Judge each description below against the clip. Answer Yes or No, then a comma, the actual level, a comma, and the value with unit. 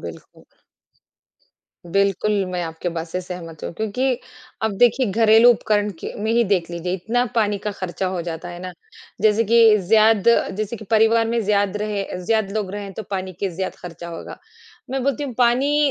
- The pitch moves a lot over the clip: No, average, 3.7 semitones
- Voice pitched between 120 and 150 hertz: No, high, 210 Hz